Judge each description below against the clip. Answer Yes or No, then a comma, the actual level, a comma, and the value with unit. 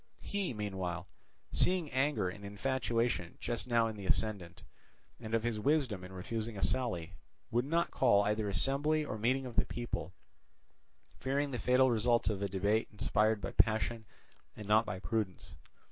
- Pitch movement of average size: Yes, average, 4.0 semitones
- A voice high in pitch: No, low, 110 Hz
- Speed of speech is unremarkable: Yes, average, 160 wpm